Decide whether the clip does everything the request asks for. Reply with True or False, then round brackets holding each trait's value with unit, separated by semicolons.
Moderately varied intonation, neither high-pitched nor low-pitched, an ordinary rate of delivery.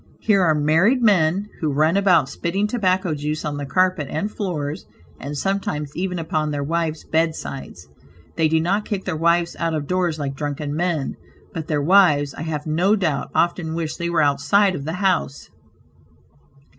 True (3.6 semitones; 160 Hz; 175 wpm)